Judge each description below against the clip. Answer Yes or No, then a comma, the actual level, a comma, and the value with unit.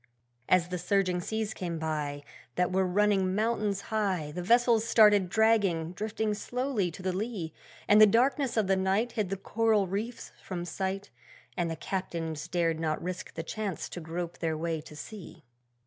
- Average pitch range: Yes, average, 4.1 semitones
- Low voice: No, high, 190 Hz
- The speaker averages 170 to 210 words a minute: Yes, average, 175 wpm